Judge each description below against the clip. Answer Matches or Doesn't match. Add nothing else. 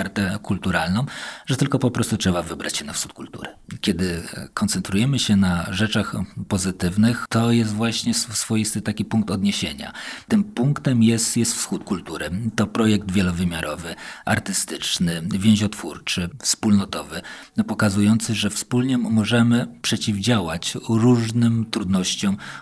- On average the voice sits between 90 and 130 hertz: Matches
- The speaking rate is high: Doesn't match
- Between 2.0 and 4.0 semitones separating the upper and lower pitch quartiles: Matches